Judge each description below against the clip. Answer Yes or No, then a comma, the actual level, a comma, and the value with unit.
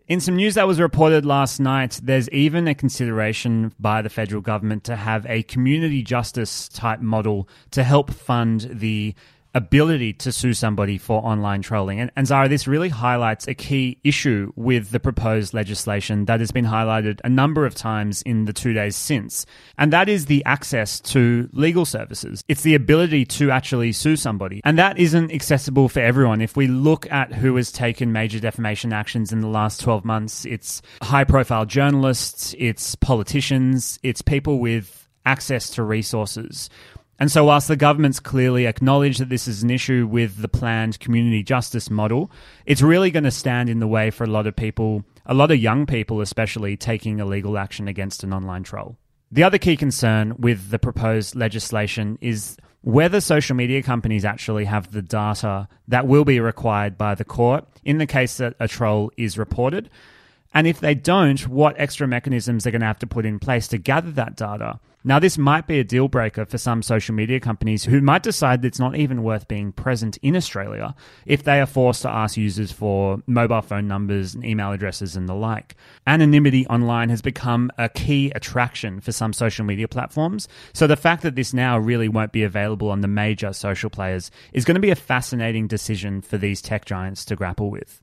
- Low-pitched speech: Yes, low, 120 Hz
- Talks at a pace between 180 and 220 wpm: Yes, average, 195 wpm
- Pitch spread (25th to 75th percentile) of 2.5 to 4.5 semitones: Yes, average, 4.1 semitones